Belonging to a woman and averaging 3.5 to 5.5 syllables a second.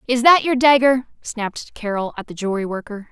No: female; 5.9 syllables/s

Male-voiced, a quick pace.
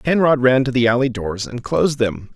Yes: male; fast, 230 wpm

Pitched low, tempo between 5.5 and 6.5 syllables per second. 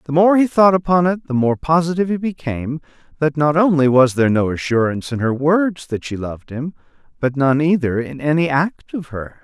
No: medium, 150 Hz; 5.6 syllables/s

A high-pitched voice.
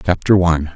No: very low, 85 Hz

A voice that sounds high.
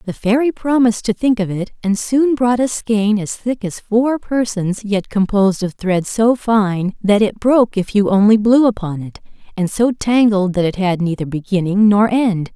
Yes: high, 210 Hz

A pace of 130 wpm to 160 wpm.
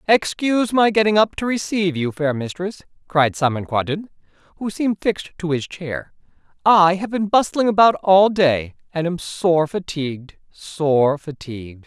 Yes: average, 150 wpm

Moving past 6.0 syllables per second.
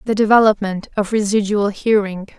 No: 5.3 syllables/s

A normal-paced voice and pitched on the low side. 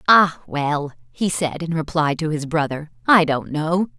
No: average, 180 wpm; medium, 155 Hz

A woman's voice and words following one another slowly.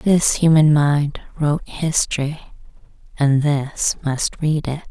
Yes: female; slow, 120 wpm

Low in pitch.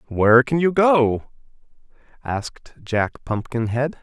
Yes: low, 130 Hz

